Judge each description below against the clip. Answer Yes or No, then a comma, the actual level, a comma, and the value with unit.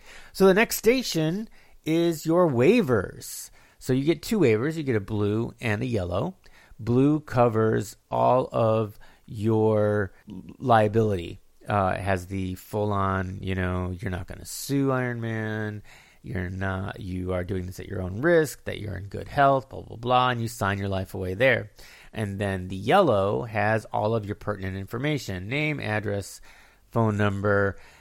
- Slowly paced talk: No, average, 170 wpm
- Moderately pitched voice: No, low, 105 Hz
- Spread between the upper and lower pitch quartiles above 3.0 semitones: Yes, average, 4.4 semitones